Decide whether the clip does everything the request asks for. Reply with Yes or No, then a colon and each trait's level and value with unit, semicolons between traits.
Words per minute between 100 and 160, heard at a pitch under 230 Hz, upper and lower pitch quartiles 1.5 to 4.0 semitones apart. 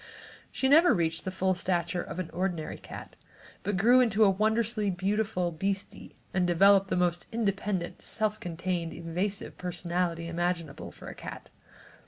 Yes: average, 155 wpm; medium, 185 Hz; average, 3.0 semitones